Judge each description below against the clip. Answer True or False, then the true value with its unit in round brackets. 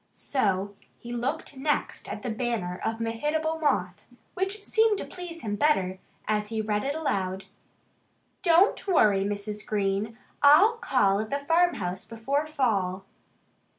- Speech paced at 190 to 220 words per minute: False (140 wpm)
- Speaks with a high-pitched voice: True (230 Hz)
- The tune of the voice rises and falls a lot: True (7.2 semitones)